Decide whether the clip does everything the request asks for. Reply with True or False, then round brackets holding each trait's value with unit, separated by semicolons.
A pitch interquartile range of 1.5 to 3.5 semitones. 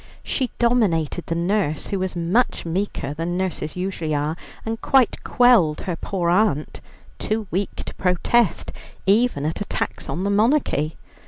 False (4.8 semitones)